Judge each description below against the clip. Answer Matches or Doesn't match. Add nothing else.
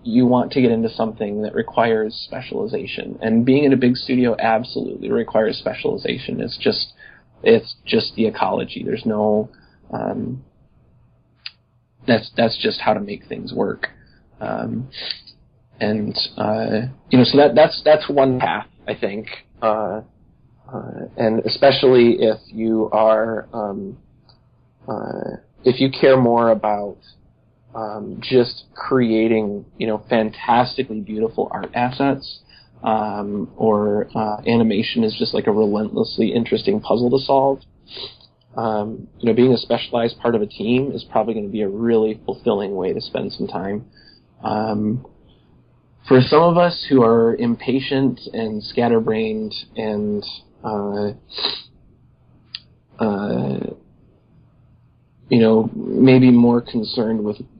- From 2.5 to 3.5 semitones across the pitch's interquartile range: Matches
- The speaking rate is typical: Doesn't match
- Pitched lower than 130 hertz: Matches